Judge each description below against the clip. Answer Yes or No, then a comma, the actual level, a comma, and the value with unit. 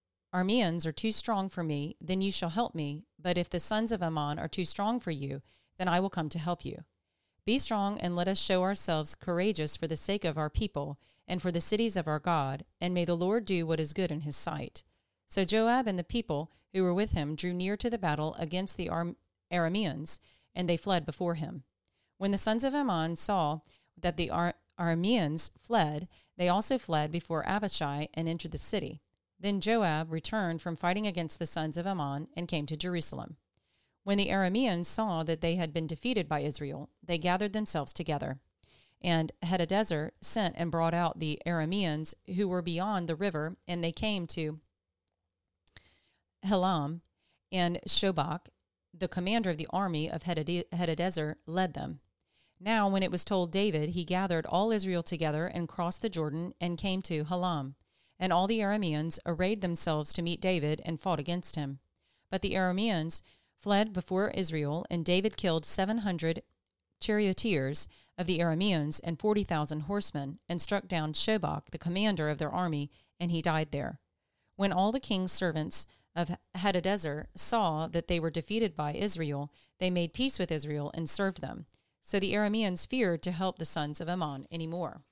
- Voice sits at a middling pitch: Yes, medium, 175 Hz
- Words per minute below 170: No, average, 180 wpm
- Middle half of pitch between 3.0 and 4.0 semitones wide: Yes, average, 3.7 semitones